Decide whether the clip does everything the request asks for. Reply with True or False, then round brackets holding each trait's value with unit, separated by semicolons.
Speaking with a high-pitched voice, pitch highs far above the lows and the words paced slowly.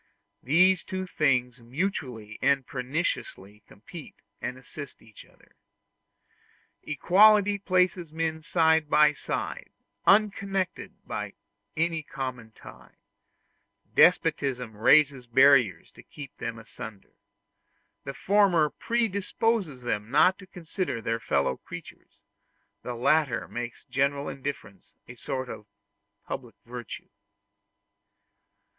False (140 Hz; 6.4 semitones; 100 wpm)